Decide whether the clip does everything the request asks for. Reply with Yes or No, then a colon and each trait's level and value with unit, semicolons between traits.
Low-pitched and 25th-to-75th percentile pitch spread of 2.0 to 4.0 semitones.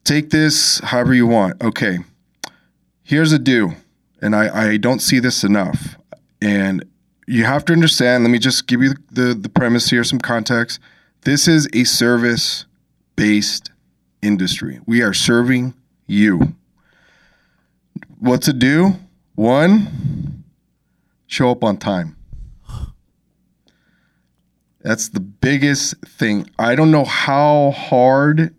No: low, 125 Hz; average, 4.5 semitones